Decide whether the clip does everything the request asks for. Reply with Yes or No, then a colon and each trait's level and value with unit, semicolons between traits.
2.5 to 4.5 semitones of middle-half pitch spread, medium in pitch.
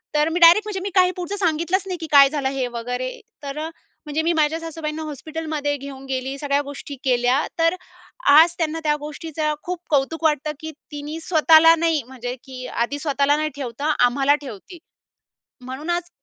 No: average, 3.0 semitones; very high, 300 Hz